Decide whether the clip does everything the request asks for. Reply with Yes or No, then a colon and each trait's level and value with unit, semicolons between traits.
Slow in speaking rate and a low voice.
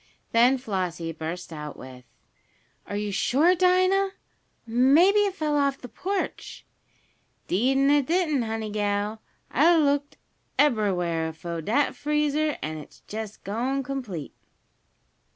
No: slow, 130 wpm; high, 245 Hz